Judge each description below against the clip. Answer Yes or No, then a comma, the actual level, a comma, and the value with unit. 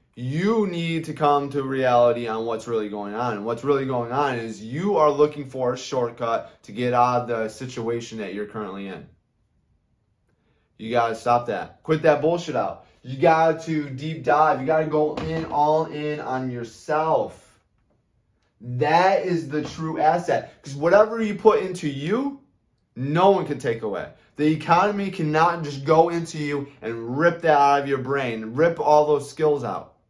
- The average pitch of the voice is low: No, medium, 145 Hz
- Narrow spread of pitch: No, average, 5.1 semitones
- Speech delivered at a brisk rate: No, average, 175 wpm